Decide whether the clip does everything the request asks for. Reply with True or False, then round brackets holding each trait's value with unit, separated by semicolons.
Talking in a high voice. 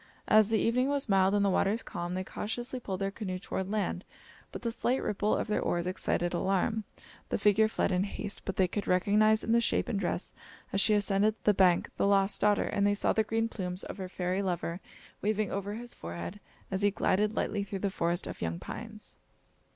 True (200 Hz)